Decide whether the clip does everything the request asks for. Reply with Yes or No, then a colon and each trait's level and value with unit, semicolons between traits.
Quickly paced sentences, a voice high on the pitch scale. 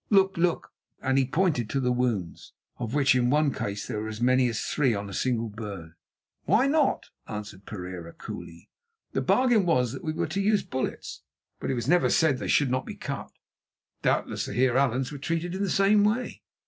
No: fast, 210 wpm; low, 130 Hz